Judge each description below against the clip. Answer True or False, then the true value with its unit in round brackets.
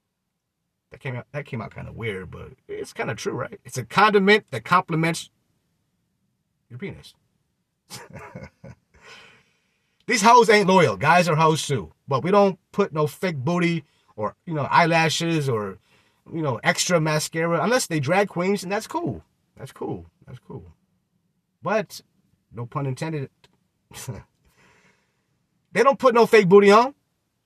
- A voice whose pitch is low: False (170 Hz)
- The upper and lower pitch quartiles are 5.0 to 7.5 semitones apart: True (5.3 semitones)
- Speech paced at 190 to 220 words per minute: False (150 wpm)